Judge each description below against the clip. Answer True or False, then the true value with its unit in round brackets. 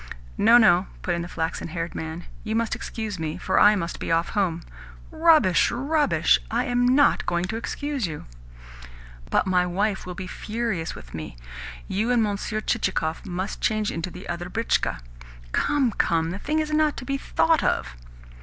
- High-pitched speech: True (200 Hz)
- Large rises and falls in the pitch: True (5.8 semitones)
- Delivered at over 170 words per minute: True (180 wpm)